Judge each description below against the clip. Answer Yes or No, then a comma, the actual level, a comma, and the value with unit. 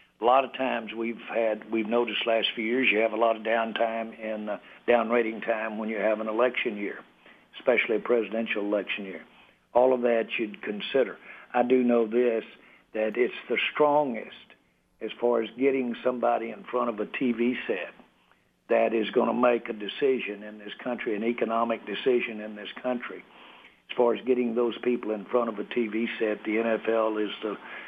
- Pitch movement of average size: No, narrow, 1.8 semitones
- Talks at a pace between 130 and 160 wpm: No, average, 190 wpm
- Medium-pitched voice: No, low, 115 Hz